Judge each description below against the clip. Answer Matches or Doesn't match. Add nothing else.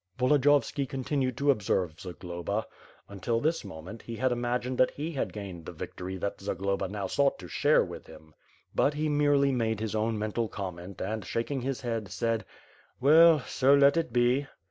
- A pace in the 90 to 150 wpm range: Doesn't match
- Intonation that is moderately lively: Doesn't match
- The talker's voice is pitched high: Doesn't match